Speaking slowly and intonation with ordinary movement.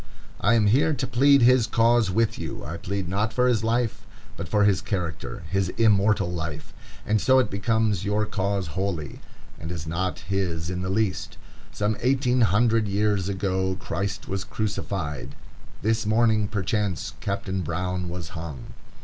No: average, 160 wpm; average, 3.4 semitones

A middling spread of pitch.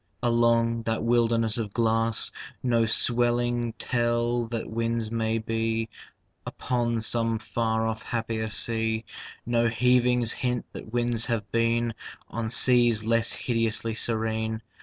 No: narrow, 1.0 semitones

